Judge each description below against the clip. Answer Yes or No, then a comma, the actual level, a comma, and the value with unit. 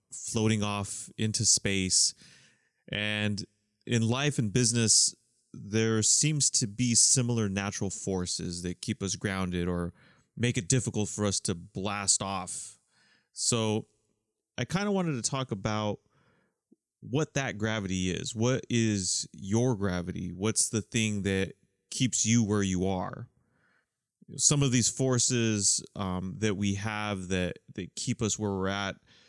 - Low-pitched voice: Yes, low, 110 Hz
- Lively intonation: No, average, 3.6 semitones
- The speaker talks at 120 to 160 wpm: Yes, average, 140 wpm